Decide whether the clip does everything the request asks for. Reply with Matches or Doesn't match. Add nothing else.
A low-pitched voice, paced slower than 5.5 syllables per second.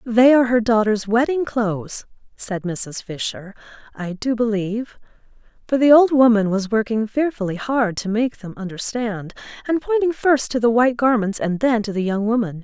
Doesn't match